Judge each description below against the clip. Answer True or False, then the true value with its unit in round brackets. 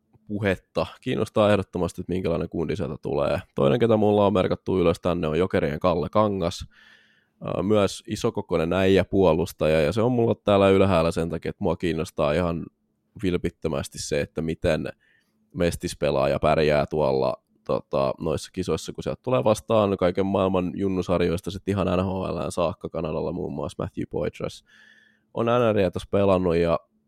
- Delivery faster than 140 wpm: True (150 wpm)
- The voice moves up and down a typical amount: True (3.2 semitones)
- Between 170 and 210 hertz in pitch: False (95 Hz)